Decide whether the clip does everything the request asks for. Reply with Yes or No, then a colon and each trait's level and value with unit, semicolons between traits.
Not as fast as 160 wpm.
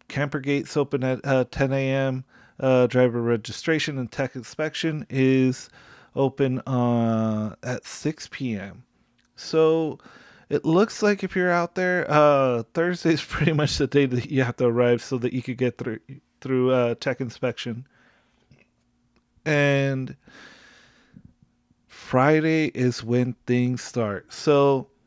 Yes: slow, 135 wpm